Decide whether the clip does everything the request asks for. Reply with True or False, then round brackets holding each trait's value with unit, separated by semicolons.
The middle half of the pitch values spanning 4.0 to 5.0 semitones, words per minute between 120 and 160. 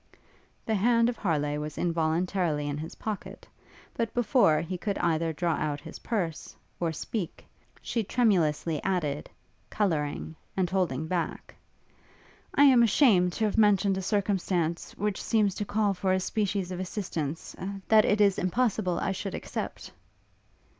True (4.4 semitones; 145 wpm)